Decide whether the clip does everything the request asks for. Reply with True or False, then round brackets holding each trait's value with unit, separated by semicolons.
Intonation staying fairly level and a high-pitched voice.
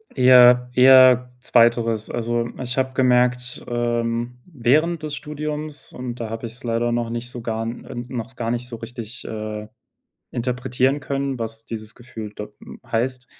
False (1.8 semitones; 120 Hz)